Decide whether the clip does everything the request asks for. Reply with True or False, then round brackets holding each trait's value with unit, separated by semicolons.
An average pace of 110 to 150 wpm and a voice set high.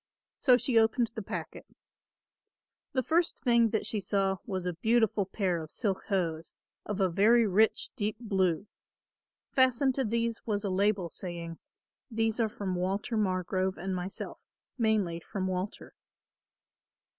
True (145 wpm; 205 Hz)